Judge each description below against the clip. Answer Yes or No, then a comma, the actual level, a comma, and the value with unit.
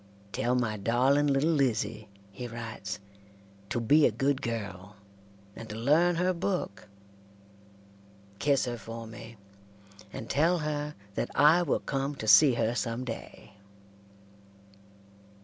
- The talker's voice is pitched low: Yes, low, 125 Hz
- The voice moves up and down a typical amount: Yes, average, 4.5 semitones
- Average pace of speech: No, slow, 130 wpm